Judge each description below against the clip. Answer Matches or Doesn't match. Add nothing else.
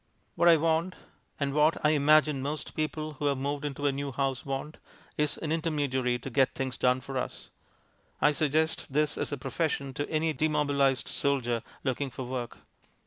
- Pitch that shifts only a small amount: Matches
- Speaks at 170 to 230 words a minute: Matches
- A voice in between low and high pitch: Matches